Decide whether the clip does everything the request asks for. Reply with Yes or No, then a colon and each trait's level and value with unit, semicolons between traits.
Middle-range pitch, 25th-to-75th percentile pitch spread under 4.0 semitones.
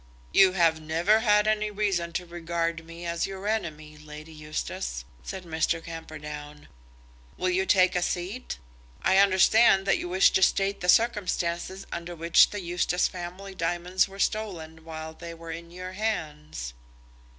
Yes: medium, 175 Hz; average, 2.9 semitones